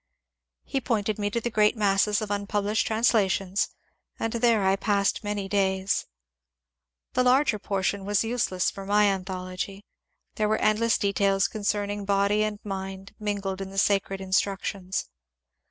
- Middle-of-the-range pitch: No, high, 205 Hz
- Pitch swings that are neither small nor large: No, narrow, 1.6 semitones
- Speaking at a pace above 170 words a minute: No, average, 145 wpm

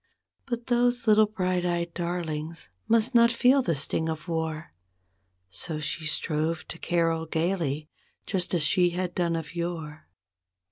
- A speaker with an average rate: Yes, average, 145 wpm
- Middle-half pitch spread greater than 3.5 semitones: No, average, 3.1 semitones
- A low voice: No, medium, 170 Hz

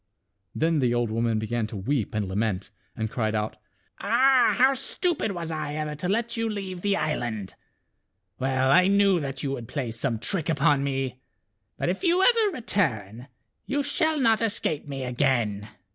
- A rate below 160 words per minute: No, average, 175 wpm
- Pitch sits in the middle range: Yes, medium, 145 Hz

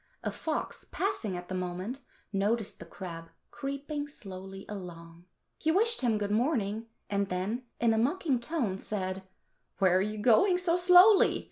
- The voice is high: Yes, high, 215 Hz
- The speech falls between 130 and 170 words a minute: Yes, average, 155 wpm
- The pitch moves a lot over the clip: Yes, wide, 7.5 semitones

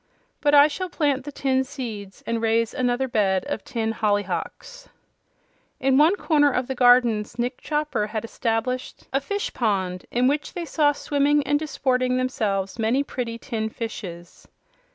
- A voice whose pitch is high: Yes, very high, 250 Hz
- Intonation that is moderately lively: Yes, average, 4.6 semitones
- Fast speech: No, average, 155 wpm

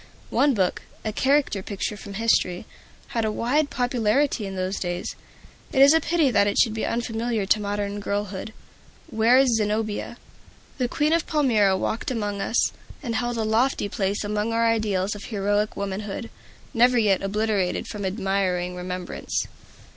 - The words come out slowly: No, average, 155 wpm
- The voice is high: Yes, high, 215 Hz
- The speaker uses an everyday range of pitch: Yes, average, 3.2 semitones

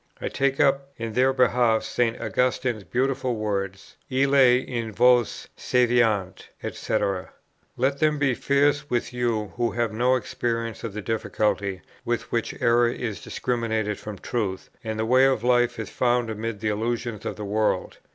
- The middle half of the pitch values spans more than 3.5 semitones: No, narrow, 2.6 semitones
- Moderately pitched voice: No, low, 120 Hz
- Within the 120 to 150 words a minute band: No, average, 160 wpm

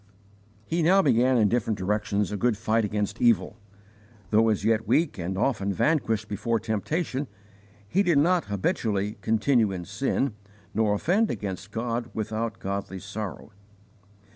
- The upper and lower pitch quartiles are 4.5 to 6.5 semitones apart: No, average, 3.3 semitones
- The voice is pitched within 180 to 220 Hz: No, low, 110 Hz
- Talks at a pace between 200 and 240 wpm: No, average, 140 wpm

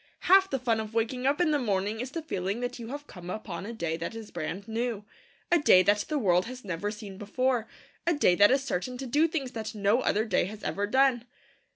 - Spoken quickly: Yes, fast, 240 wpm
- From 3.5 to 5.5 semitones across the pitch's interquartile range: Yes, average, 4.5 semitones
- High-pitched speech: Yes, high, 225 Hz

